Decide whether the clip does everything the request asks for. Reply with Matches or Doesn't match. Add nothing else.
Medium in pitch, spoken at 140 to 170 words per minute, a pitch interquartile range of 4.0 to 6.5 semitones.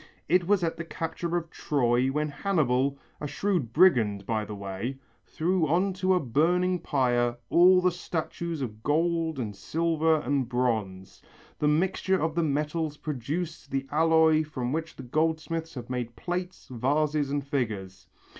Matches